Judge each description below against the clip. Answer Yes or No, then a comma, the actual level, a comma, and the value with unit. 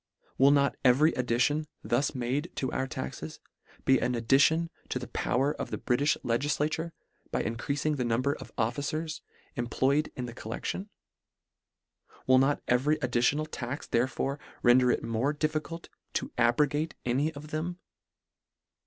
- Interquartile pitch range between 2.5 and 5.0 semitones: Yes, average, 3.6 semitones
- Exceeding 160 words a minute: No, average, 155 wpm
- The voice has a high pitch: No, low, 135 Hz